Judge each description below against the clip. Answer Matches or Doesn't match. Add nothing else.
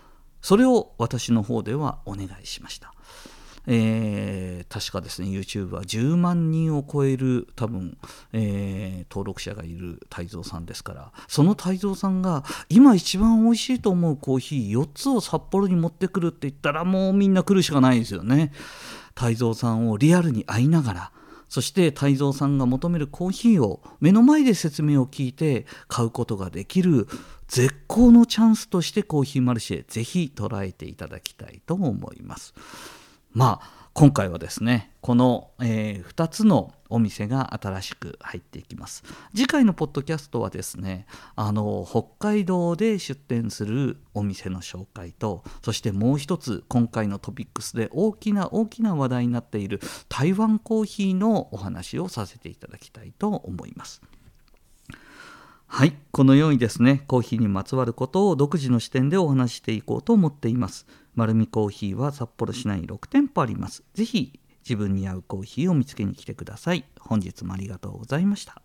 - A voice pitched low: Matches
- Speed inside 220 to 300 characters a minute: Doesn't match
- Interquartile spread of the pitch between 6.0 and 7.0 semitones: Doesn't match